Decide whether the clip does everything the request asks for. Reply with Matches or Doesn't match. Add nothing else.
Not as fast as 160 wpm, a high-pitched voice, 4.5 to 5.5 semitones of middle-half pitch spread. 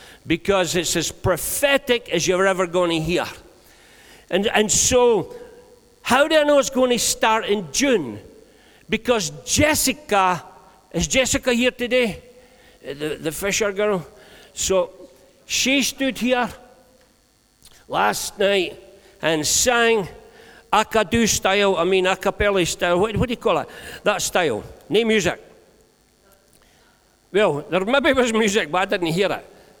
Matches